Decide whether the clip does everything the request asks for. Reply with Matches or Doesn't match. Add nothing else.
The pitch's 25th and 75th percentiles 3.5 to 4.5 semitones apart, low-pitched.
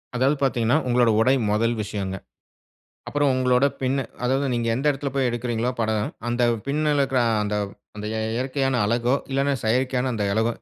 Doesn't match